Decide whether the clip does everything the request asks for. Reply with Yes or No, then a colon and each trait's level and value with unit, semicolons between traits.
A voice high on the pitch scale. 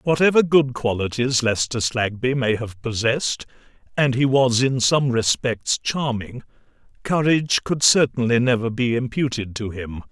No: low, 125 Hz